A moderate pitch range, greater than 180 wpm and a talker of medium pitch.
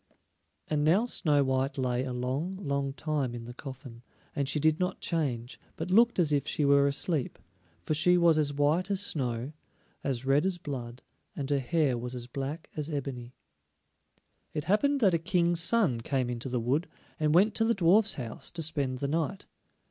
Yes: average, 4.4 semitones; average, 190 wpm; medium, 145 Hz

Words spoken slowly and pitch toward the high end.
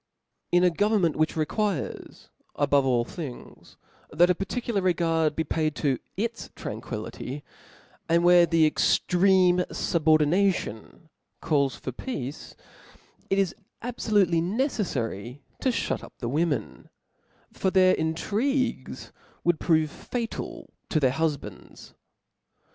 No: slow, 115 wpm; medium, 165 Hz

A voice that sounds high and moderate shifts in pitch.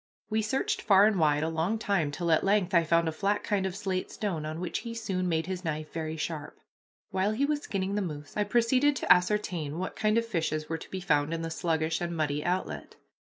No: medium, 180 Hz; average, 4.5 semitones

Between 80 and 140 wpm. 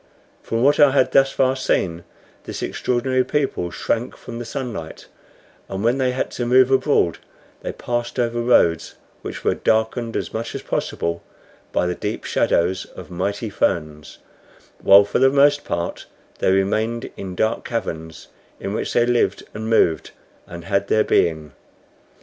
No: average, 160 wpm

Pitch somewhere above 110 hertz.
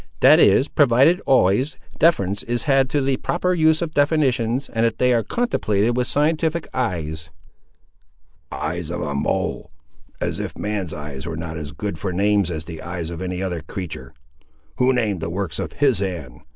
No: low, 105 Hz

